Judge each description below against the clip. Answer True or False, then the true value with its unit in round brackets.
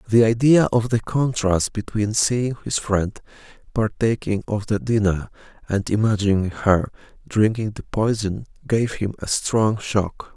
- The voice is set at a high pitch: False (110 Hz)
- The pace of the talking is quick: False (140 wpm)